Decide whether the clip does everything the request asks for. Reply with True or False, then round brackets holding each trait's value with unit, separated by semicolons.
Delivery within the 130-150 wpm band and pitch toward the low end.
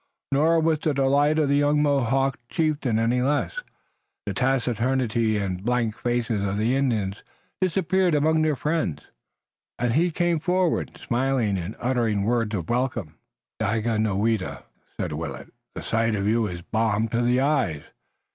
True (145 wpm; 120 Hz)